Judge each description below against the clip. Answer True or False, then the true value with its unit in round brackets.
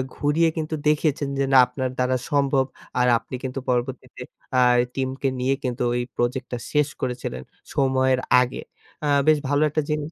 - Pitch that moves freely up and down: False (2.4 semitones)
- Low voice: True (130 Hz)